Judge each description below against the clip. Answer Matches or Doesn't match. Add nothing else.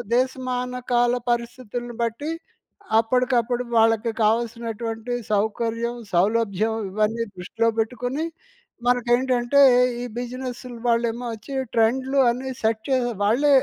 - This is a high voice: Matches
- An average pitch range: Doesn't match